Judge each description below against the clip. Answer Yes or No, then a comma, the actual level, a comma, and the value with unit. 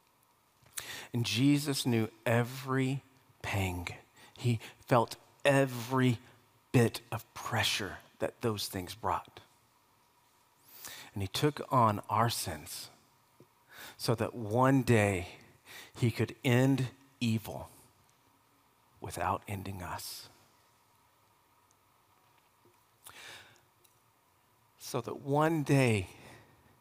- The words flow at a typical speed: No, slow, 80 wpm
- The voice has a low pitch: Yes, low, 120 Hz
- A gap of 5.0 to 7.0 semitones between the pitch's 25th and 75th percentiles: No, average, 2.9 semitones